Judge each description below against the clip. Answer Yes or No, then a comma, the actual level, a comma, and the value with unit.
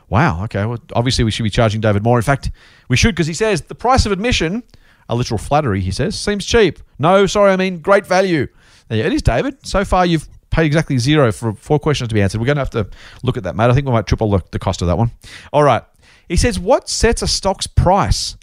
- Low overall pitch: Yes, low, 125 Hz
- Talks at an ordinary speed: No, fast, 255 wpm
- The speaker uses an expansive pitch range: Yes, wide, 7.9 semitones